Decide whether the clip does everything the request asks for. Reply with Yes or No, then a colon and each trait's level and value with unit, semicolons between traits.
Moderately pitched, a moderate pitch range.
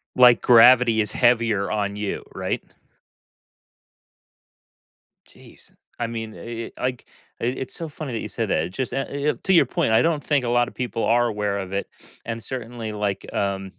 No: low, 115 Hz; average, 3.2 semitones